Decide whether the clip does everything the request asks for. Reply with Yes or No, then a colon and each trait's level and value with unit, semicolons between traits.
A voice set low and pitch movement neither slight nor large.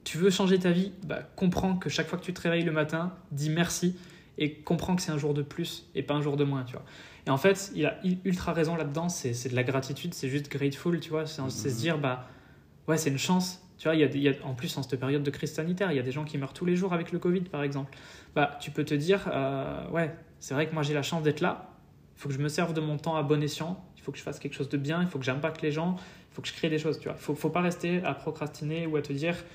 No: medium, 155 Hz; average, 3.2 semitones